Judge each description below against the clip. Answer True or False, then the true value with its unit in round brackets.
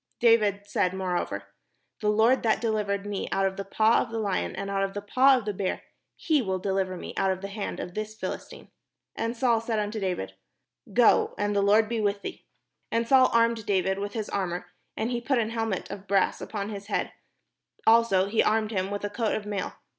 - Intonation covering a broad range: False (2.5 semitones)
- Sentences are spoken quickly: True (220 wpm)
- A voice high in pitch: True (205 Hz)